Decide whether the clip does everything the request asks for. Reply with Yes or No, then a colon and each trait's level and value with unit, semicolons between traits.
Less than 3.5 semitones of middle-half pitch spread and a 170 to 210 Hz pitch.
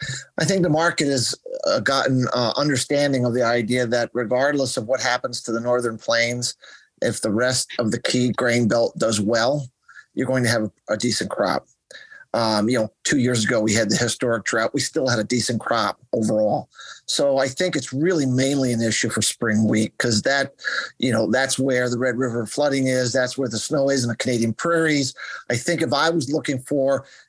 No: narrow, 2.6 semitones; low, 125 Hz